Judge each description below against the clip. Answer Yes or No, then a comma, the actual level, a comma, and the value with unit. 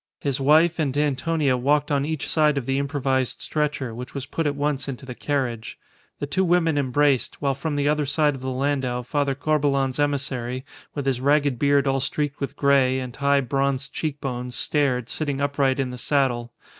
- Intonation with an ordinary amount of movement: No, narrow, 1.9 semitones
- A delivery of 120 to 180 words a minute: No, average, 195 wpm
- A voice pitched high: No, medium, 140 Hz